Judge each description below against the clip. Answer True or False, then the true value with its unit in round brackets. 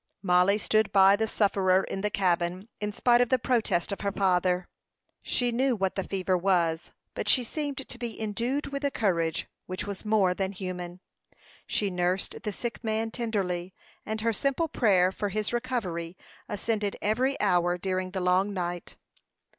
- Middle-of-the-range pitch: False (200 Hz)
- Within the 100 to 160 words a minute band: False (170 wpm)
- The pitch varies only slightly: False (3.7 semitones)